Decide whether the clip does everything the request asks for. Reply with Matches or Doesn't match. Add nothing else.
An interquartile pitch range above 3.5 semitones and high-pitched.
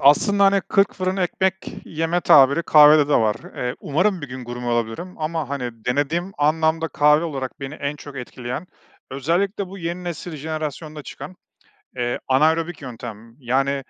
Doesn't match